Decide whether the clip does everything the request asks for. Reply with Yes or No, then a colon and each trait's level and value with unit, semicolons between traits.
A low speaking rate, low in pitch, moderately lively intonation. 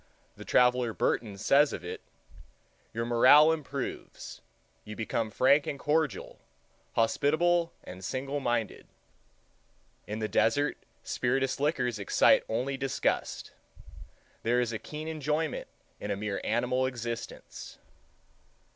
Yes: slow, 110 wpm; low, 125 Hz; average, 4.3 semitones